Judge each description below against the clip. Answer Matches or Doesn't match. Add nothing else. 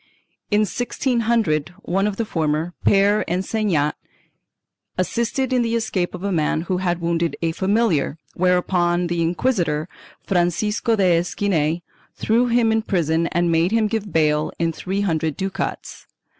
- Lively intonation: Doesn't match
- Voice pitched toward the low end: Doesn't match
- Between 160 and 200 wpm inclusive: Doesn't match